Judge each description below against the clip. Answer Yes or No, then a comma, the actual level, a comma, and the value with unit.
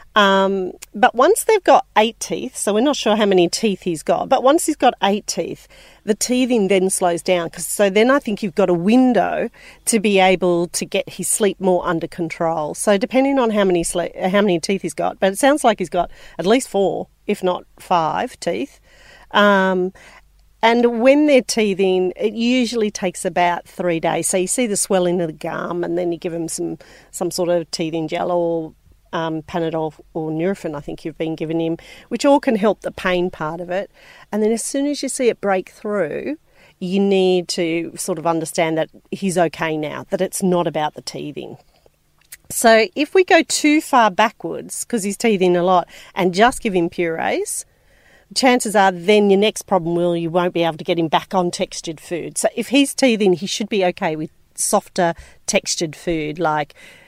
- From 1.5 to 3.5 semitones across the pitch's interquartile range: No, average, 4.2 semitones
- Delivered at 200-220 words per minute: Yes, fast, 205 wpm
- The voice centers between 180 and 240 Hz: Yes, medium, 185 Hz